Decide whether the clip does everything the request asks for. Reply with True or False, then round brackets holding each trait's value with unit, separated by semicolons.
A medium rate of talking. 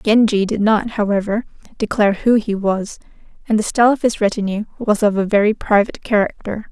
True (180 wpm)